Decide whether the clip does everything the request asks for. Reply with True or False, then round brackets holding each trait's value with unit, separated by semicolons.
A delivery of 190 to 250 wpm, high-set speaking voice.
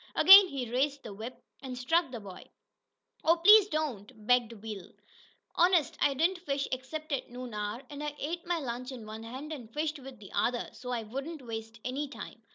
True (195 wpm; 260 Hz)